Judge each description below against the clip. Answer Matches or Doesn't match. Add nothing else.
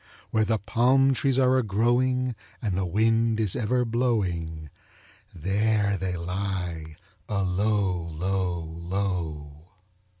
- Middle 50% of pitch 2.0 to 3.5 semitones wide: Doesn't match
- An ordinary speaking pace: Doesn't match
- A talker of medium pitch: Doesn't match